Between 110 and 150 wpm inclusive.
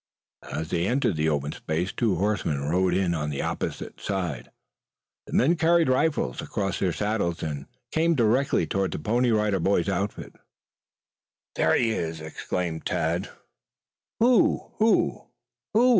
Yes: average, 145 wpm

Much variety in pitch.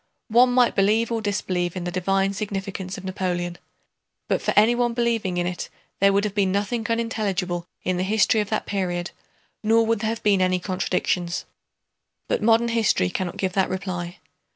No: average, 3.3 semitones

